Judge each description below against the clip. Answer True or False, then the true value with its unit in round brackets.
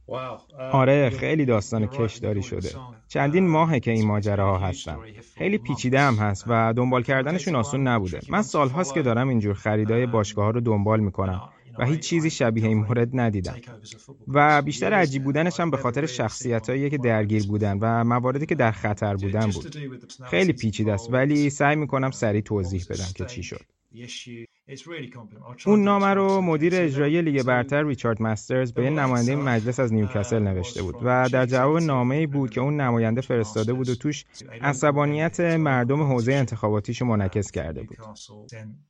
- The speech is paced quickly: True (165 wpm)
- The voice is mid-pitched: False (125 Hz)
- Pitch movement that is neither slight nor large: True (4.5 semitones)